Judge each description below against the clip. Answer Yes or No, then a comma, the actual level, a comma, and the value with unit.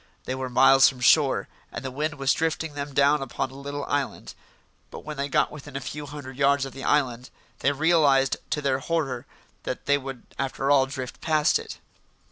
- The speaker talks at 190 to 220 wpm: Yes, average, 200 wpm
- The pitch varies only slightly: Yes, narrow, 1.8 semitones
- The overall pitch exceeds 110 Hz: Yes, medium, 140 Hz